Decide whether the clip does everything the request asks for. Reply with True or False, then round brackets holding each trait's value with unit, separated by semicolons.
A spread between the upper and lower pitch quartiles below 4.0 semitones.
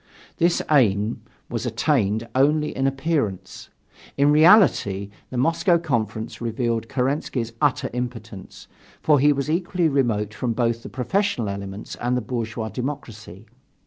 False (4.9 semitones)